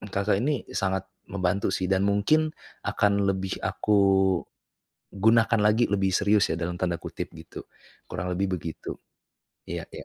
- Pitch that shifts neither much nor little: No, narrow, 2.0 semitones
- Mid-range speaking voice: No, low, 100 Hz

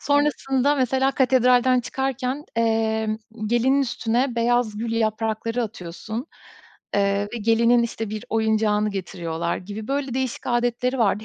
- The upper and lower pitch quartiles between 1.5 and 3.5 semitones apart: Yes, average, 2.9 semitones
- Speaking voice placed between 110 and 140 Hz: No, high, 230 Hz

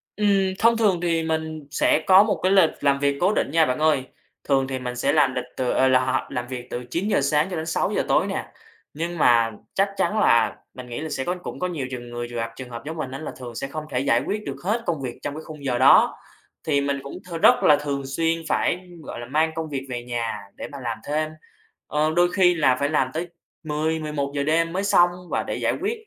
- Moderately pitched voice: Yes, medium, 150 Hz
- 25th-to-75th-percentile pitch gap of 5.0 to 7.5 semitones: No, average, 4.3 semitones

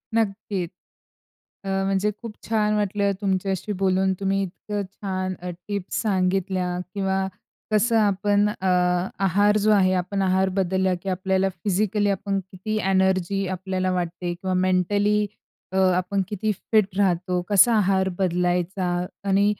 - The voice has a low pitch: No, high, 195 Hz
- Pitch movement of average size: No, narrow, 1.7 semitones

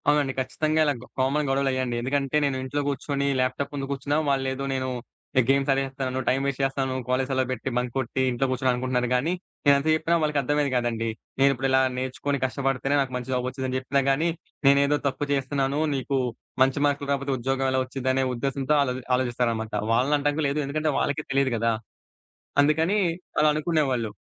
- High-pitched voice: No, low, 135 Hz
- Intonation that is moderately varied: No, narrow, 1.6 semitones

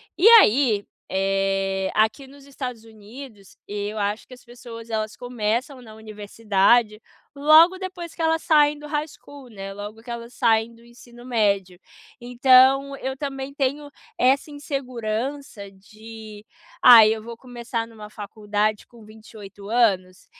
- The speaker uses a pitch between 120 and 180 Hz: No, high, 230 Hz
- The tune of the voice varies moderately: Yes, average, 4.1 semitones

